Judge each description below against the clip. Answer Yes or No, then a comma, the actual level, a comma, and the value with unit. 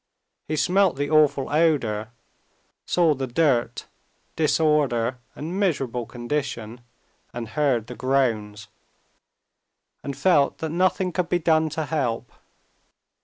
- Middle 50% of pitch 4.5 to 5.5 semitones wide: Yes, average, 4.9 semitones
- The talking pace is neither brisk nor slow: No, slow, 115 wpm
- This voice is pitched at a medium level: Yes, medium, 145 Hz